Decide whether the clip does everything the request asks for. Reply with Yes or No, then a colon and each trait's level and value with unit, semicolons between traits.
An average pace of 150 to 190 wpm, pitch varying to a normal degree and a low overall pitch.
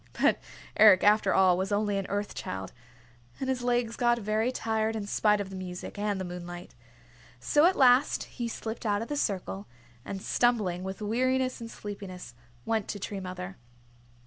No: average, 175 wpm; average, 3.6 semitones; high, 205 Hz